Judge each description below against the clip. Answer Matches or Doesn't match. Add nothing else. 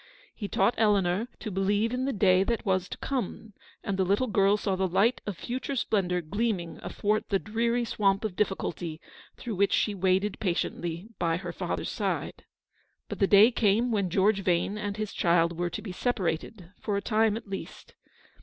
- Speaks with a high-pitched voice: Matches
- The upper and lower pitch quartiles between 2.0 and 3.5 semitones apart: Matches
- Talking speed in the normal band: Matches